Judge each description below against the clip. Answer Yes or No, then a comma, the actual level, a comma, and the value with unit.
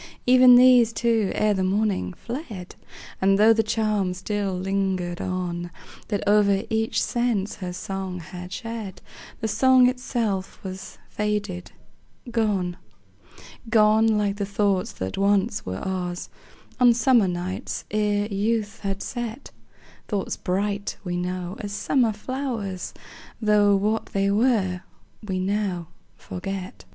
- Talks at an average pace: No, slow, 125 wpm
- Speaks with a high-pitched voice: Yes, high, 205 Hz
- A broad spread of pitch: No, average, 2.9 semitones